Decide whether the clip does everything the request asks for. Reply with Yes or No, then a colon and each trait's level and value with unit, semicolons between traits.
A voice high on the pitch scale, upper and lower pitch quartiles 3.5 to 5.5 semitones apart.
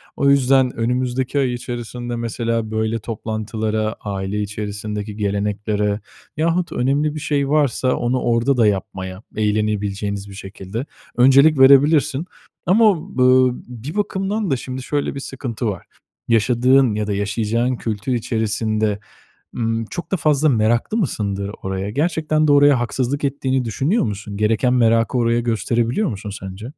No: low, 120 Hz; average, 4.2 semitones